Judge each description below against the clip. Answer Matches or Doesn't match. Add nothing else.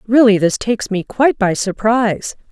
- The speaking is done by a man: Doesn't match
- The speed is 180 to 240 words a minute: Doesn't match